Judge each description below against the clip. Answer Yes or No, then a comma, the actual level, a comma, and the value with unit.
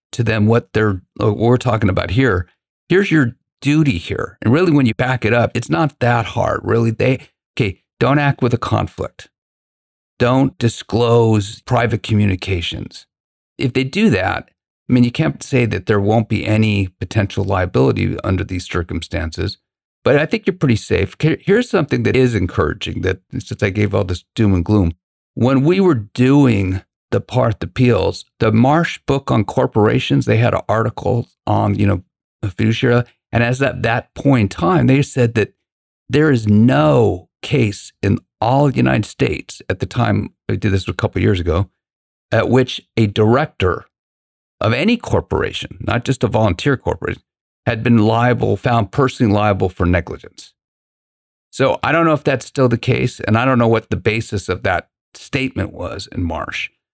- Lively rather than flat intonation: No, average, 4.2 semitones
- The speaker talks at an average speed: Yes, average, 175 wpm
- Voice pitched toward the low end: Yes, low, 115 Hz